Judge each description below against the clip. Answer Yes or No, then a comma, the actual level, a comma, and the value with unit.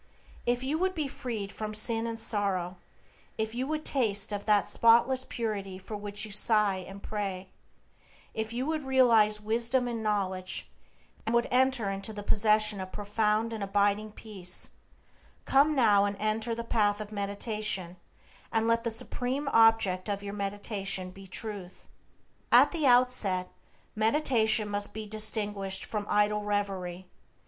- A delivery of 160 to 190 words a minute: No, average, 150 wpm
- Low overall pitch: No, high, 215 Hz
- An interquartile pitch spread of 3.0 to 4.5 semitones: No, narrow, 2.5 semitones